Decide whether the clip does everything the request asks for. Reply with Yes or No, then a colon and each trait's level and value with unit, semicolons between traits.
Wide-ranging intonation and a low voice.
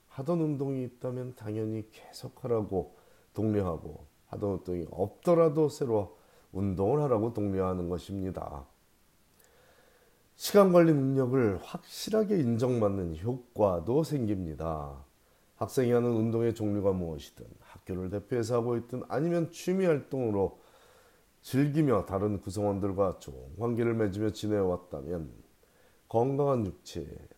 Yes: wide, 5.7 semitones; low, 110 Hz